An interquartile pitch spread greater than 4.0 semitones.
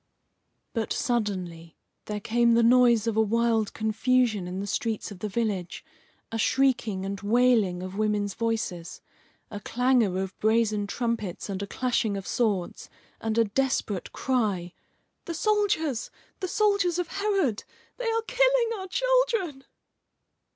Yes: average, 4.6 semitones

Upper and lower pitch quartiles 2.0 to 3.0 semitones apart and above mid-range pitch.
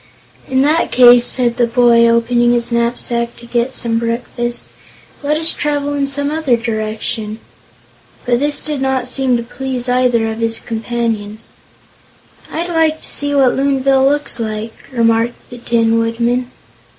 Yes: narrow, 2.5 semitones; high, 240 Hz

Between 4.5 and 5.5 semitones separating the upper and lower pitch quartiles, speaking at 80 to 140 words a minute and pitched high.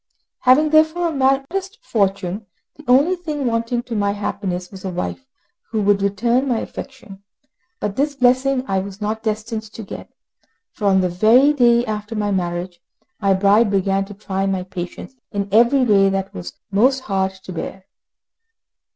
No: average, 4.8 semitones; average, 170 wpm; high, 210 Hz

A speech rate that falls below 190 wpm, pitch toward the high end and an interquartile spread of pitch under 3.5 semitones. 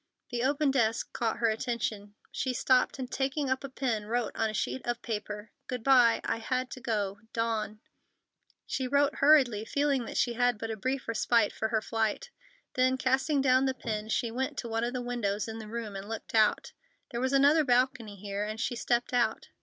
No: average, 200 wpm; high, 240 Hz; average, 2.9 semitones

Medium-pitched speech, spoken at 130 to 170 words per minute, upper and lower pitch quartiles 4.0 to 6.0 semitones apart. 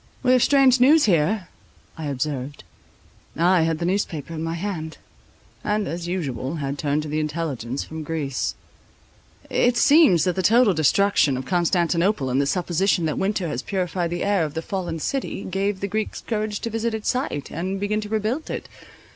No: medium, 175 Hz; average, 180 wpm; average, 5.1 semitones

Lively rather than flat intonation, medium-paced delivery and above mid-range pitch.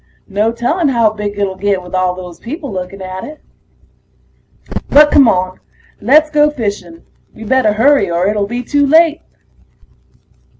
Yes: wide, 7.2 semitones; average, 155 wpm; high, 215 Hz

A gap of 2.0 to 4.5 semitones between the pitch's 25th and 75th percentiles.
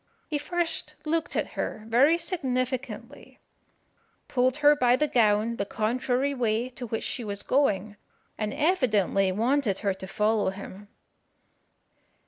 No: average, 5.1 semitones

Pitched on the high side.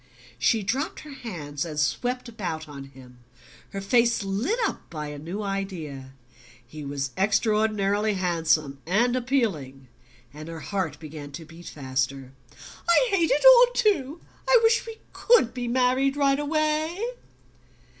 Yes: high, 195 Hz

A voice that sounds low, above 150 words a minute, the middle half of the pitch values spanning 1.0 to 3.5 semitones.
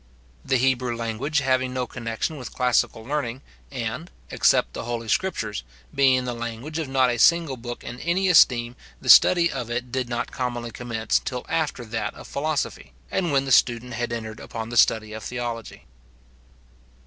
Yes: low, 125 Hz; average, 170 wpm; narrow, 2.6 semitones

